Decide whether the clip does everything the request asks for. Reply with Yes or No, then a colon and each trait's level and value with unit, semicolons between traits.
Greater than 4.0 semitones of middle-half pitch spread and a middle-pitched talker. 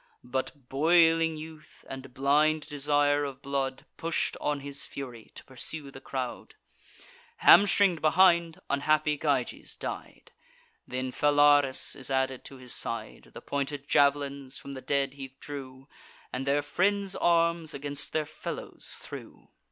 No: narrow, 2.5 semitones; medium, 145 Hz